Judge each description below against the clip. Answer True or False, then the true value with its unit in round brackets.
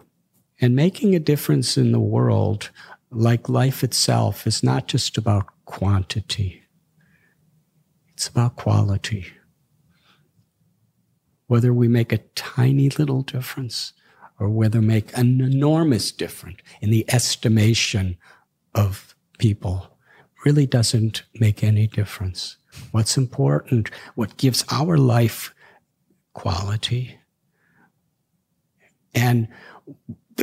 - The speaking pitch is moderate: False (120 Hz)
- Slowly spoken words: True (95 wpm)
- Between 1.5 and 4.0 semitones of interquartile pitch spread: True (3.7 semitones)